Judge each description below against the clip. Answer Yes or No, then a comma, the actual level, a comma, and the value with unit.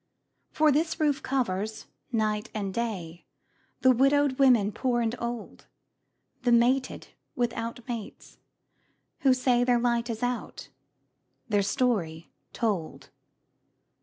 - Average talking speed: No, slow, 110 wpm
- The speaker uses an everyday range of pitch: Yes, average, 3.2 semitones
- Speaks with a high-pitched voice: Yes, high, 235 Hz